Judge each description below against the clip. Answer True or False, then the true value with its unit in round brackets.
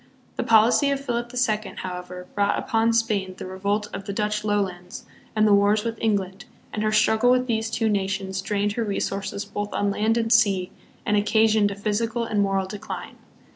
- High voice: True (210 Hz)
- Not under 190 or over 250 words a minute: True (195 wpm)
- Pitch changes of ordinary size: False (2.1 semitones)